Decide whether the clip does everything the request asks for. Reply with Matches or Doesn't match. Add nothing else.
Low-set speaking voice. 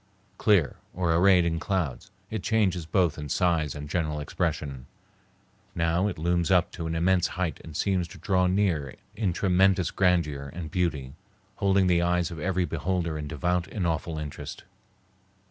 Matches